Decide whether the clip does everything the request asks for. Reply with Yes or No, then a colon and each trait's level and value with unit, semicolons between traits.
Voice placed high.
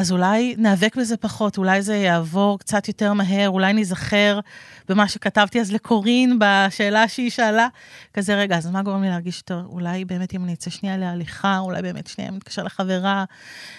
Yes: high, 200 Hz